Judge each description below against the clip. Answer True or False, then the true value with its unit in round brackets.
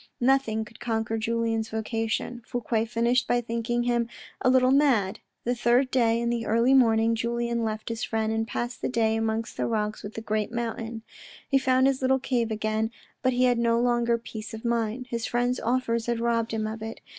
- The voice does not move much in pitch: True (1.5 semitones)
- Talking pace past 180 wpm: True (200 wpm)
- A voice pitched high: True (230 Hz)